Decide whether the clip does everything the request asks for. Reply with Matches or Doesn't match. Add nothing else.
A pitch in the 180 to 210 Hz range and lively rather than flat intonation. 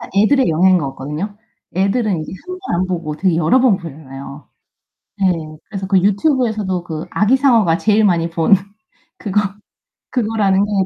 Doesn't match